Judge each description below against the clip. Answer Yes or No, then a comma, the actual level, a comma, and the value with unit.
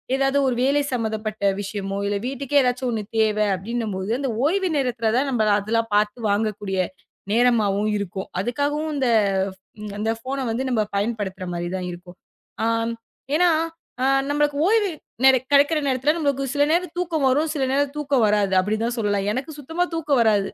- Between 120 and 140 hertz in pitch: No, high, 240 Hz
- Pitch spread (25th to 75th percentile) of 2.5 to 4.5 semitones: No, average, 5.3 semitones